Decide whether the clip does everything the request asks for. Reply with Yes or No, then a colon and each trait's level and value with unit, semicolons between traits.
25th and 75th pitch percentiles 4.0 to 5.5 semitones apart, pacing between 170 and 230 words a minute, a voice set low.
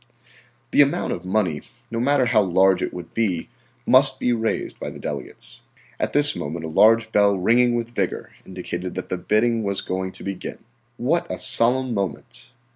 Yes: average, 4.5 semitones; average, 180 wpm; low, 110 Hz